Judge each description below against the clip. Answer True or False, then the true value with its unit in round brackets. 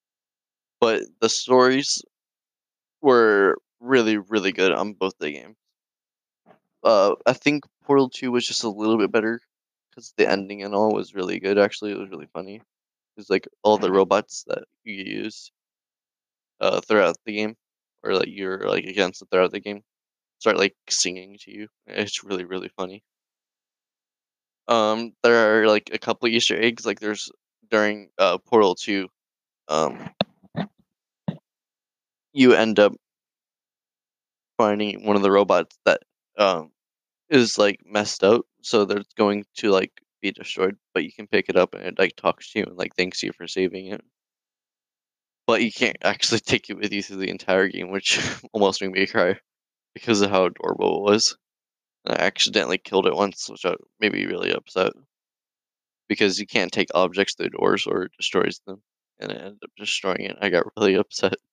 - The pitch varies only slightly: True (2.3 semitones)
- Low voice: True (105 Hz)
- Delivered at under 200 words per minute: True (170 wpm)